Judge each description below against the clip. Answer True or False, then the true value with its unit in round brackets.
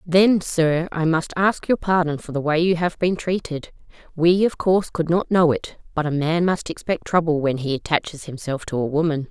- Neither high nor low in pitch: True (165 Hz)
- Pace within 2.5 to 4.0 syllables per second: False (5.0 syllables/s)